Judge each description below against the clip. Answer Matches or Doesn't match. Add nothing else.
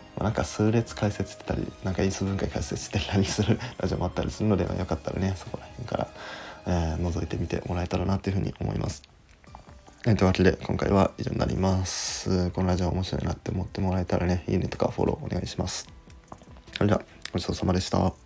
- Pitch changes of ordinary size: Doesn't match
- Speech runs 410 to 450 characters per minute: Matches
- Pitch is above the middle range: Doesn't match